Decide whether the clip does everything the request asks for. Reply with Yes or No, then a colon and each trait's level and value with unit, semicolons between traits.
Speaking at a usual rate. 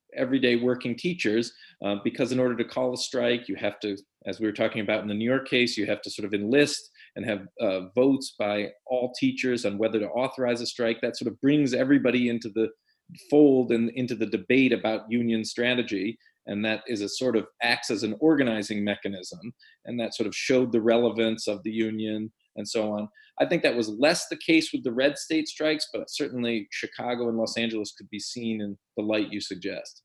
No: fast, 215 wpm